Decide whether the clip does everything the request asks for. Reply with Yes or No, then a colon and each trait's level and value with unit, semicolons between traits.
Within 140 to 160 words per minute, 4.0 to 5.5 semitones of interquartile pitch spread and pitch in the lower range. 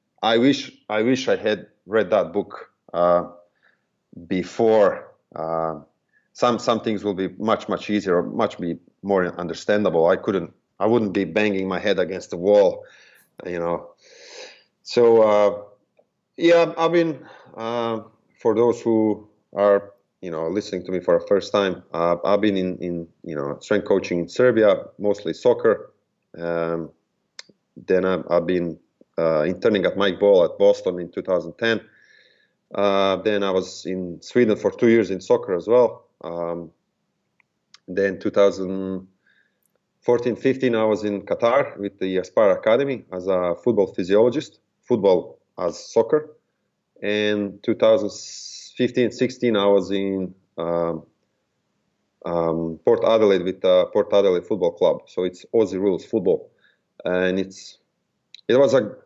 Yes: average, 145 wpm; average, 4.8 semitones; low, 100 Hz